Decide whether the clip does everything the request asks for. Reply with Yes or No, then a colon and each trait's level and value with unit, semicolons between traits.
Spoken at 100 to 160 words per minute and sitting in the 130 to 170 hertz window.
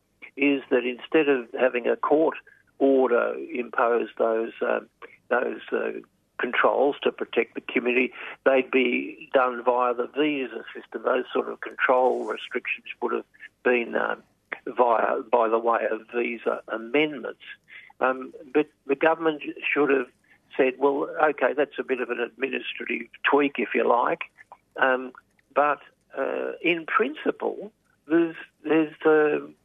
Yes: average, 140 wpm; low, 135 Hz